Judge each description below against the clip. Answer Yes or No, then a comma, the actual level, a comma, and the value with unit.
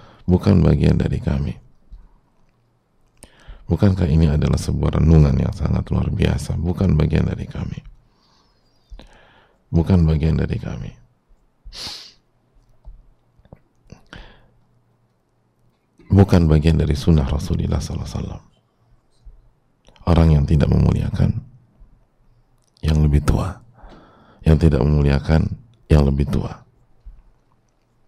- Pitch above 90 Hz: No, very low, 85 Hz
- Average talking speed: No, slow, 90 wpm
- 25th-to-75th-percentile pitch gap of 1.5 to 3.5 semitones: No, wide, 5.5 semitones